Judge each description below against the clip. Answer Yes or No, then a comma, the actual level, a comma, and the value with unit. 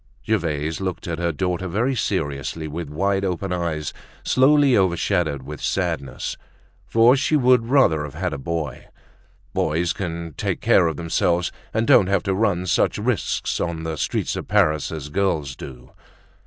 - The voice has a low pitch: Yes, very low, 85 Hz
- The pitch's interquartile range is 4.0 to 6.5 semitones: Yes, average, 4.3 semitones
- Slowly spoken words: No, average, 160 wpm